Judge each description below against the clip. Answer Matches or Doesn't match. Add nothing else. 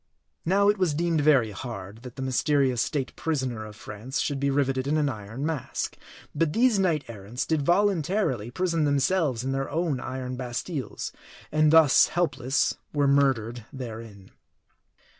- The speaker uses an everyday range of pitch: Matches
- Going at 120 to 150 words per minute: Doesn't match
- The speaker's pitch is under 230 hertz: Matches